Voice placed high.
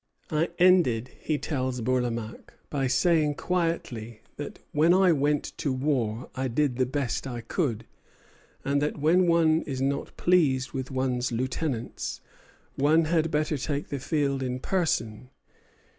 No: medium, 140 Hz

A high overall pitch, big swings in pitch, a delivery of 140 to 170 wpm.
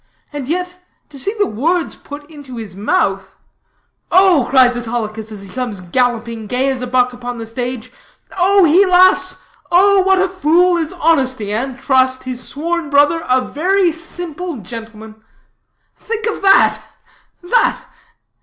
Yes: very high, 270 Hz; wide, 6.7 semitones; average, 145 wpm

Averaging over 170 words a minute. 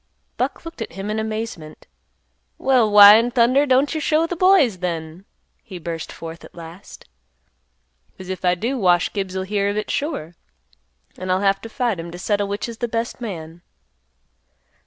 Yes: average, 180 wpm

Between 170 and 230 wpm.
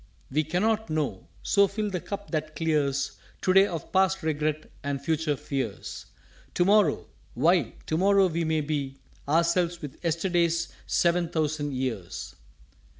No: average, 145 wpm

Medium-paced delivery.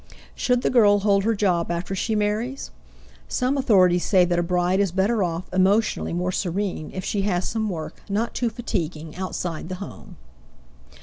Yes: average, 175 wpm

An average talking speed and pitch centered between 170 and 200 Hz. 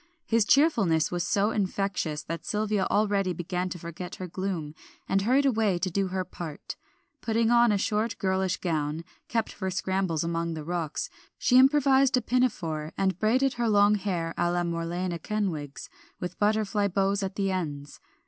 Yes: average, 165 wpm; high, 190 Hz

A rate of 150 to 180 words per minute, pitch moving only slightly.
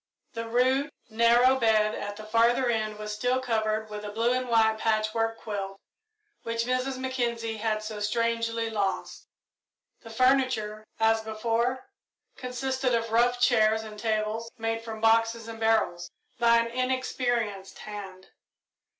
No: average, 140 wpm; narrow, 2.0 semitones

